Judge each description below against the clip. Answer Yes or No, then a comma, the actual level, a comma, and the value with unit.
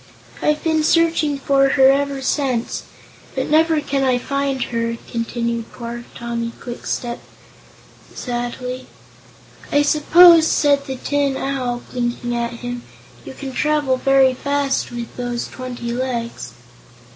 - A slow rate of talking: Yes, slow, 125 wpm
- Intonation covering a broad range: No, average, 2.9 semitones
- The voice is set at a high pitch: Yes, very high, 260 Hz